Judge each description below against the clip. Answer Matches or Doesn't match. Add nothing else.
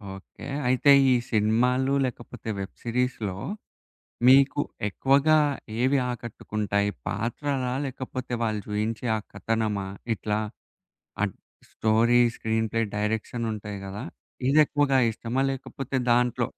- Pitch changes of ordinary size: Matches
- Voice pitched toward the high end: Doesn't match